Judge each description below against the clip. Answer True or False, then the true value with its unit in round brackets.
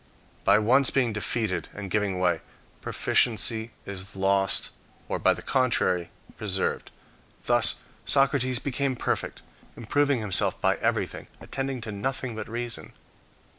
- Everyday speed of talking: False (125 wpm)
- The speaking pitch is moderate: False (110 Hz)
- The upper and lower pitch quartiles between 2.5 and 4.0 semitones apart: False (4.6 semitones)